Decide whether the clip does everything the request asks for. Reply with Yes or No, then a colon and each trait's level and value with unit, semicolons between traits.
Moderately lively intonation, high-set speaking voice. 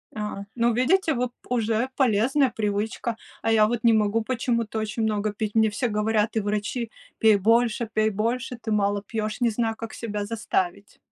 No: narrow, 1.9 semitones; high, 220 Hz